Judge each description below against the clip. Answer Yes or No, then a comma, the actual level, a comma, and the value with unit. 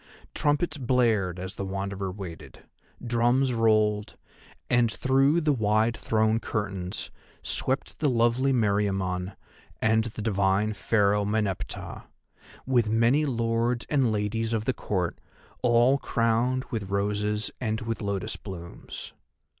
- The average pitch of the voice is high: No, low, 110 Hz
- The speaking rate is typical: No, slow, 120 wpm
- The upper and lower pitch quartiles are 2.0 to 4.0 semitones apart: Yes, average, 3.1 semitones